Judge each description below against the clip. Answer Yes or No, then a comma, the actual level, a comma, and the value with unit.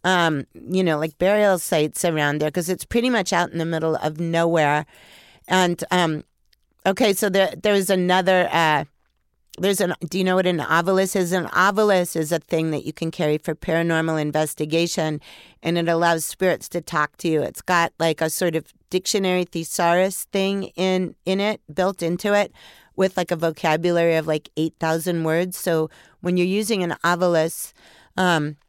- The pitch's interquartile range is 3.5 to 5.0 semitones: No, average, 2.7 semitones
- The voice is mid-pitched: Yes, medium, 170 Hz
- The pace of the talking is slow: No, average, 180 wpm